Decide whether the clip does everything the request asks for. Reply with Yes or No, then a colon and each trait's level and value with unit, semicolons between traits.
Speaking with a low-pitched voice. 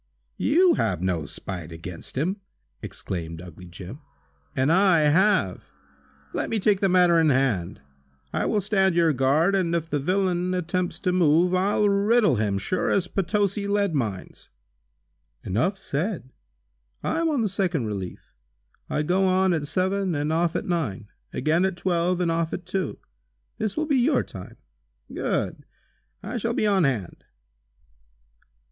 No: medium, 175 Hz